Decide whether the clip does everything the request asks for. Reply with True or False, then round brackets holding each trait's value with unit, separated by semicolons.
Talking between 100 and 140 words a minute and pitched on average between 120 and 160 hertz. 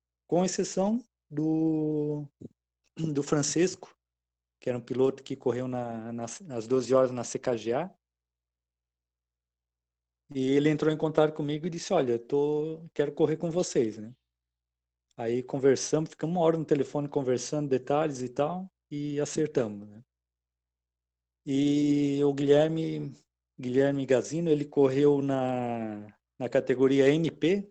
True (130 wpm; 135 Hz)